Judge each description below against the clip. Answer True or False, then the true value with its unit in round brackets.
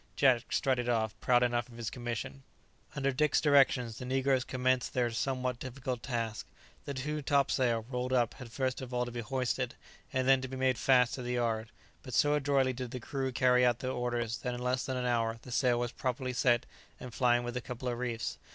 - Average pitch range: False (1.5 semitones)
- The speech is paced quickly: True (215 wpm)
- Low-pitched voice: True (125 Hz)